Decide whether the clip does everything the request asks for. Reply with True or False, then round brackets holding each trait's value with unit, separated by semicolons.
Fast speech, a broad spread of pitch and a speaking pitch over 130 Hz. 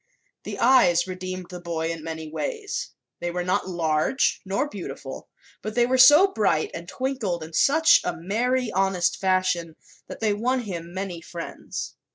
False (165 wpm; 6.4 semitones; 185 Hz)